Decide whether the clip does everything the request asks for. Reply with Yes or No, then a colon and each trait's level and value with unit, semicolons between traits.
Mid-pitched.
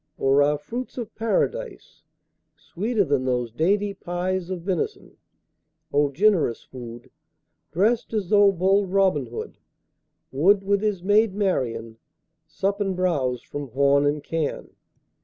Yes: medium, 180 Hz